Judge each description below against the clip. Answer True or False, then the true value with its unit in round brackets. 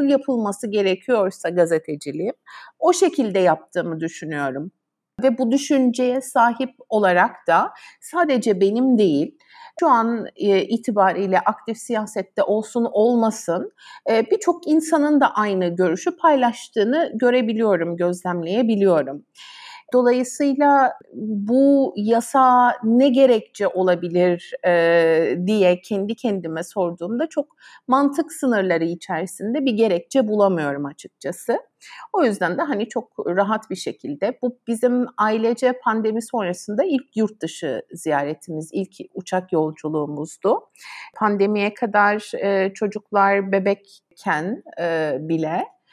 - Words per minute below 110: True (100 wpm)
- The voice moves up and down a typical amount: False (5.7 semitones)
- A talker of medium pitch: False (215 Hz)